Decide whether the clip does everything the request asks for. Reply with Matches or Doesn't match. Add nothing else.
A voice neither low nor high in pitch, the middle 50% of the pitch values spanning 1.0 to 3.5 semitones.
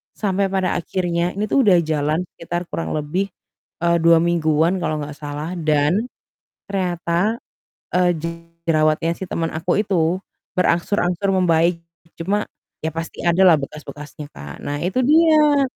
Matches